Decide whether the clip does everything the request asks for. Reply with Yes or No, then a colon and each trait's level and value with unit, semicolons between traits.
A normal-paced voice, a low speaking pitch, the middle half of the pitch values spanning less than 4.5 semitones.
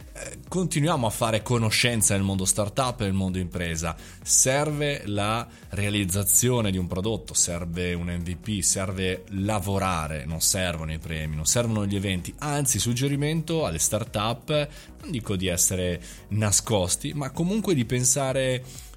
No: average, 135 wpm; low, 100 Hz; wide, 5.6 semitones